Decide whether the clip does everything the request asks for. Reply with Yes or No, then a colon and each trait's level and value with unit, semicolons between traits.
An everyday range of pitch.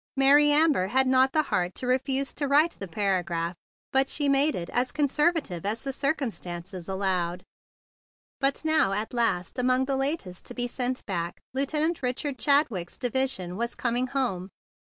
No: wide, 6.5 semitones